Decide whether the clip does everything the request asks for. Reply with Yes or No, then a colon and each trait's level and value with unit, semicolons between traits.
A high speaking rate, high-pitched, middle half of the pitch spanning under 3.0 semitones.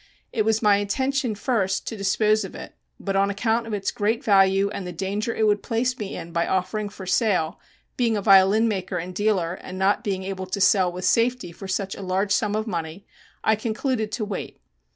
Yes: fast, 215 wpm; high, 200 Hz; narrow, 2.5 semitones